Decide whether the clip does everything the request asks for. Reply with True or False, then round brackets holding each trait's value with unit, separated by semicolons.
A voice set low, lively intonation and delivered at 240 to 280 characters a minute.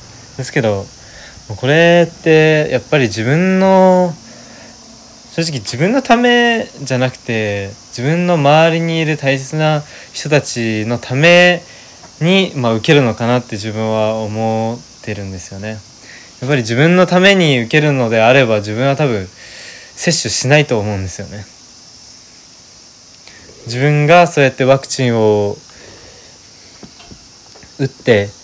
True (130 Hz; 6.2 semitones; 250 characters per minute)